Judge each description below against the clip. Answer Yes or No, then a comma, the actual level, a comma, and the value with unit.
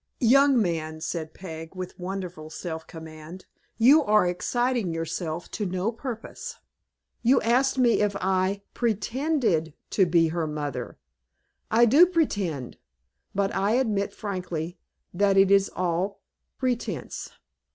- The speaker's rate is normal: No, slow, 125 wpm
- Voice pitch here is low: No, high, 195 Hz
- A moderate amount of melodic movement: No, wide, 5.7 semitones